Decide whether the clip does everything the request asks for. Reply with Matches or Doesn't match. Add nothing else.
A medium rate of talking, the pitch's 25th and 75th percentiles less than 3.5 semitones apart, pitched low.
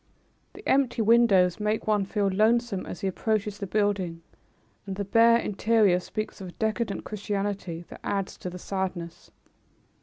Doesn't match